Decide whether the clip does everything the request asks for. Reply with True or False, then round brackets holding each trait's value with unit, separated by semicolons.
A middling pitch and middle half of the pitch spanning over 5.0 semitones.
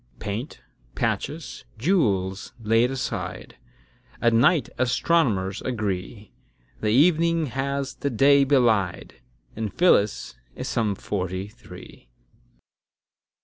False (115 Hz; 5.6 semitones)